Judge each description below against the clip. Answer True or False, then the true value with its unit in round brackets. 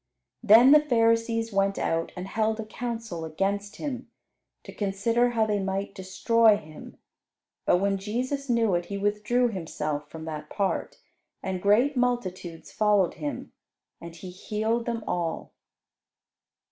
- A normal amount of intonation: True (3.7 semitones)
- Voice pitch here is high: True (210 Hz)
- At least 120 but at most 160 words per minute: True (140 wpm)